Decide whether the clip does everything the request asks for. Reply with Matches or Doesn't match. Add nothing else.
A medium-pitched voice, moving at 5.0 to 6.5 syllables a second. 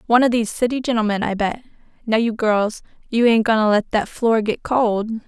Doesn't match